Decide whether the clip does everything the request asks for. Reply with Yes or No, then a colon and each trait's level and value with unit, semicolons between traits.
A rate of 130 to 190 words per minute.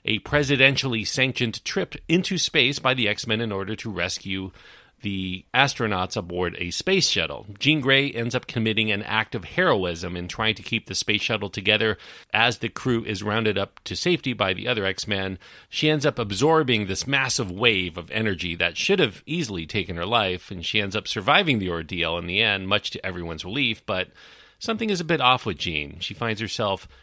No: average, 200 wpm